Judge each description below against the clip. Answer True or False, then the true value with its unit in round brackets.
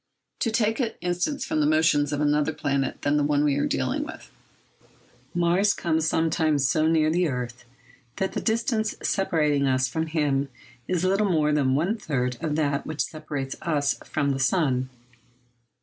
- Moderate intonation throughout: True (3.6 semitones)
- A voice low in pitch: False (155 Hz)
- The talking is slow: False (170 wpm)